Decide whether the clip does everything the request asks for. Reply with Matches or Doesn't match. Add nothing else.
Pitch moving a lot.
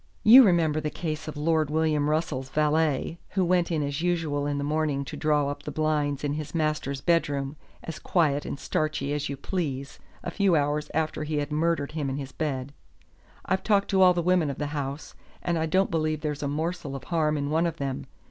Doesn't match